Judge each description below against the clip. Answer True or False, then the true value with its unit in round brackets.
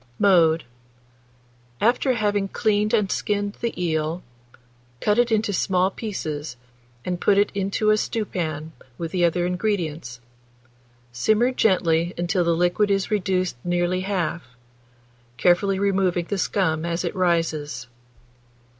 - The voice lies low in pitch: False (185 Hz)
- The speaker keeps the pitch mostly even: False (3.3 semitones)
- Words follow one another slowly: True (125 wpm)